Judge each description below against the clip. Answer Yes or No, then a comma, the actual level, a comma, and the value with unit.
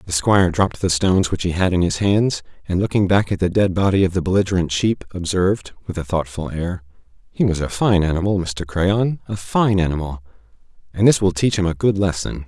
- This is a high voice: No, very low, 90 Hz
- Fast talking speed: Yes, fast, 210 wpm